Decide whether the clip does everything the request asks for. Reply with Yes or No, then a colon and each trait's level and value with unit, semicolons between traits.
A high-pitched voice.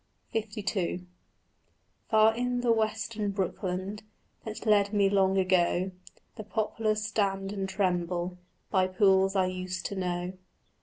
Yes: high, 195 Hz